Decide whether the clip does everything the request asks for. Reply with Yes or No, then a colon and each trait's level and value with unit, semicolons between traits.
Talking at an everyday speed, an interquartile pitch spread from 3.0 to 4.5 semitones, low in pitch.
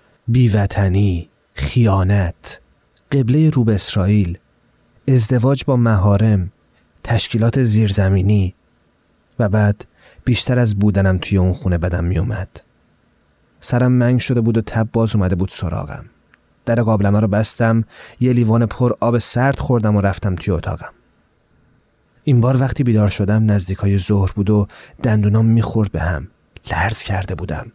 Yes: average, 130 wpm; average, 3.7 semitones; low, 105 Hz